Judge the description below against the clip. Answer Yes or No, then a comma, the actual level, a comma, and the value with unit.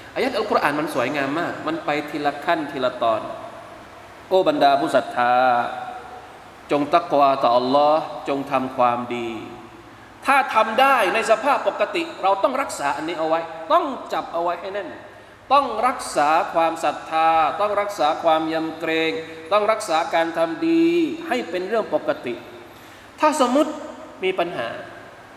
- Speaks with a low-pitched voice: No, high, 190 Hz